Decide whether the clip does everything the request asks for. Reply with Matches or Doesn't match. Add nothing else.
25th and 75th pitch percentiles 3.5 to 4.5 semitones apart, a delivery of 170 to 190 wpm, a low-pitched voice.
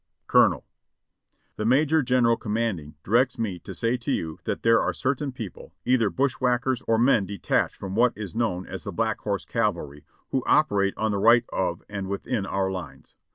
Matches